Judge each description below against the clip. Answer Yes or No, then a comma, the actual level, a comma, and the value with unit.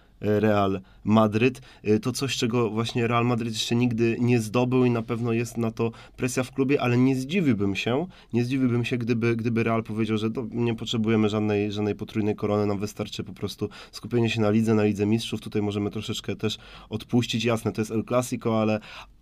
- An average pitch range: No, narrow, 2.1 semitones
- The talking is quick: Yes, fast, 190 wpm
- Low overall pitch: Yes, low, 115 Hz